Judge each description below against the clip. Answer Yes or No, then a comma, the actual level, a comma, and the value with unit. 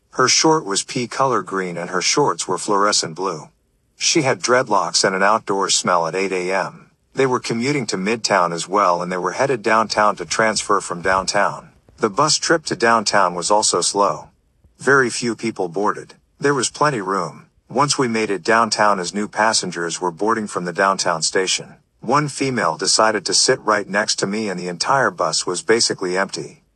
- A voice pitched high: No, low, 105 Hz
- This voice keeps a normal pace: Yes, average, 190 wpm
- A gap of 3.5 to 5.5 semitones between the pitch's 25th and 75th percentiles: Yes, average, 4.3 semitones